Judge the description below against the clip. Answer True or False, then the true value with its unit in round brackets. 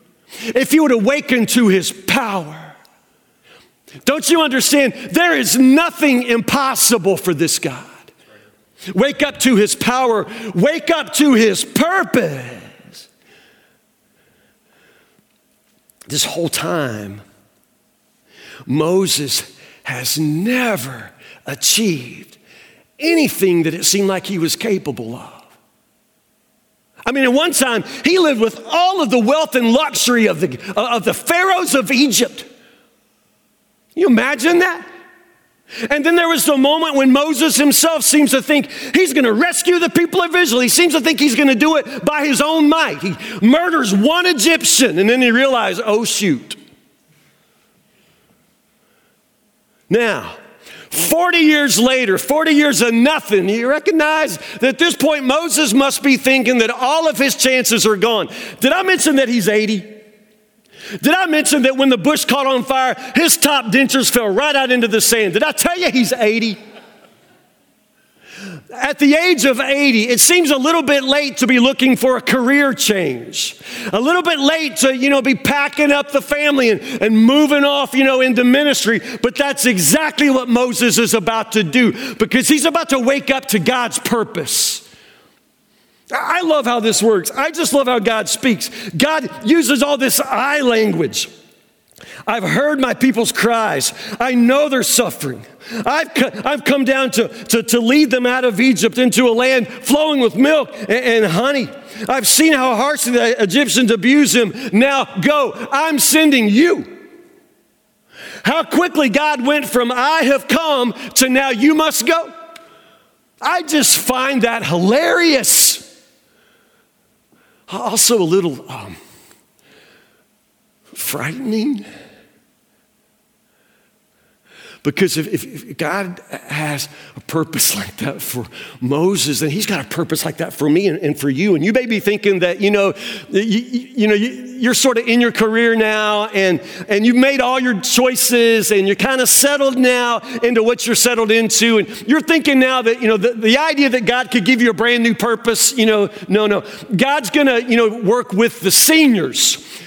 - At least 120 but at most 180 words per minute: True (160 wpm)